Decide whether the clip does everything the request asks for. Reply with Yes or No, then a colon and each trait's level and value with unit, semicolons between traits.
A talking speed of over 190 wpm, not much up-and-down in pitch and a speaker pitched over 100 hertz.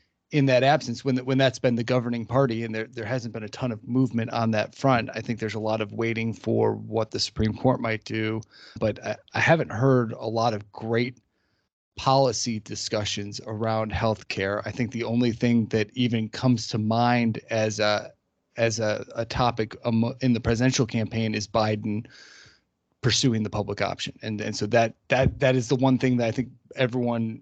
Yes: average, 200 wpm; narrow, 2.2 semitones; low, 115 Hz